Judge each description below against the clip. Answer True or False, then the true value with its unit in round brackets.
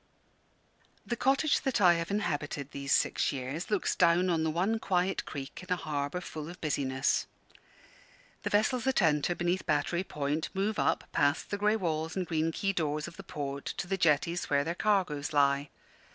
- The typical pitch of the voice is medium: True (170 Hz)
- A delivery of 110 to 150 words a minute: False (180 wpm)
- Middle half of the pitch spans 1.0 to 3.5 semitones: False (4.7 semitones)